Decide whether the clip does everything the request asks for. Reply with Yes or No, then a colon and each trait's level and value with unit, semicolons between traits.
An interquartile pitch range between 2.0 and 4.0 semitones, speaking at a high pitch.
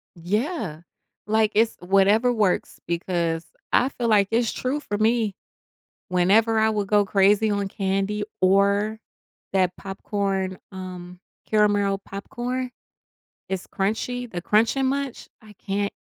Yes: narrow, 2.5 semitones; high, 205 Hz